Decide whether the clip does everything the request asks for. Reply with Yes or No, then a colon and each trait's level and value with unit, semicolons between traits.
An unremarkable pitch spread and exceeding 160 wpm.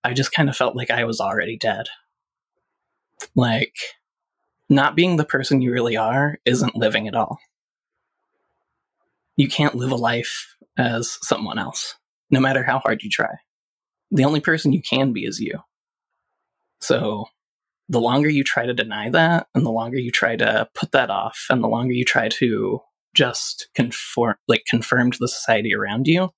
Yes: average, 3.5 semitones; average, 175 wpm